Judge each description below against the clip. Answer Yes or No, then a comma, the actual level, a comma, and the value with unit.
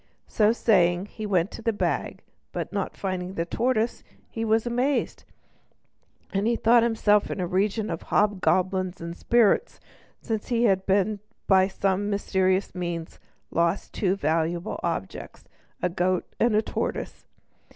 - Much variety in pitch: No, average, 3.6 semitones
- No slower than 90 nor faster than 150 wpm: Yes, average, 140 wpm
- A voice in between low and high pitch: No, high, 195 Hz